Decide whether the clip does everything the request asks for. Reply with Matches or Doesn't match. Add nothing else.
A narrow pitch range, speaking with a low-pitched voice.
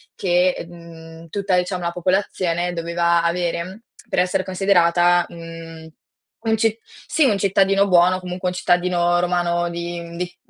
Doesn't match